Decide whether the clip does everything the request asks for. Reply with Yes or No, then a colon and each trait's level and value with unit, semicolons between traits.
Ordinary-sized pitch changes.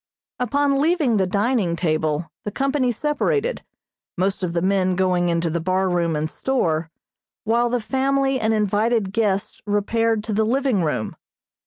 No: wide, 5.9 semitones